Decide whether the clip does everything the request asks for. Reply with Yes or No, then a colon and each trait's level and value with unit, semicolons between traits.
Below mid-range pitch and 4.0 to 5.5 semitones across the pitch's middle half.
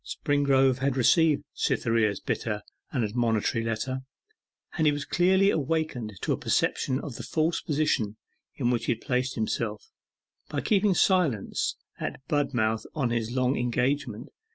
Yes: low, 130 Hz; average, 4.4 semitones